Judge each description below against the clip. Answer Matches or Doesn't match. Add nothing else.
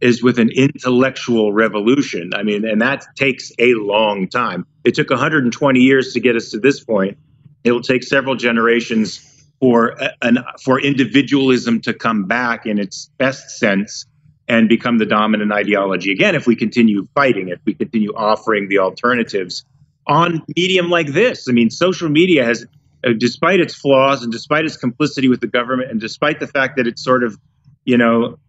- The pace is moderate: Matches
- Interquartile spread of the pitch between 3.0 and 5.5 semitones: Matches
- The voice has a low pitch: Matches